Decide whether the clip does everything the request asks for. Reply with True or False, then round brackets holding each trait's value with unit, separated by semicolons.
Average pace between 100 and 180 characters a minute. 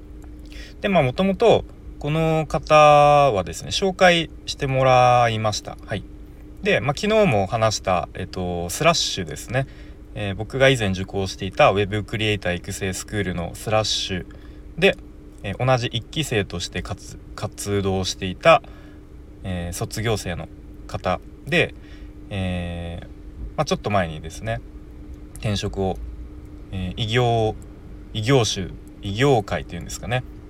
False (270 characters per minute)